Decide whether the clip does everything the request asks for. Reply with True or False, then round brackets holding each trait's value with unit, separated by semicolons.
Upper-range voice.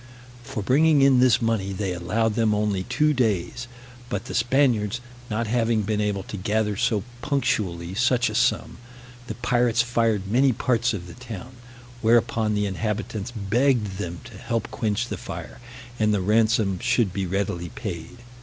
False (110 Hz)